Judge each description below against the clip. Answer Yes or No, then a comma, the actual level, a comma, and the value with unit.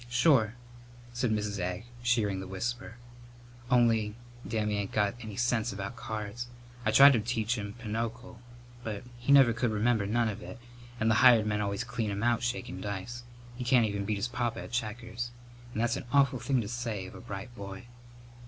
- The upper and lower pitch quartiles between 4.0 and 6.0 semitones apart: No, narrow, 2.6 semitones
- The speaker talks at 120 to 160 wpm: No, average, 190 wpm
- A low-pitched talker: Yes, low, 115 Hz